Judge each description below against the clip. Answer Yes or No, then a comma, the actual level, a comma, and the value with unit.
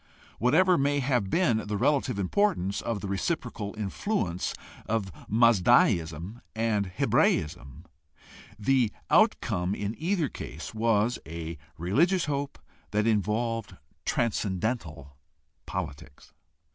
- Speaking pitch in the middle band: No, low, 110 Hz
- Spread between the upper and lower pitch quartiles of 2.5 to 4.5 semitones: No, average, 5.3 semitones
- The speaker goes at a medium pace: No, slow, 105 wpm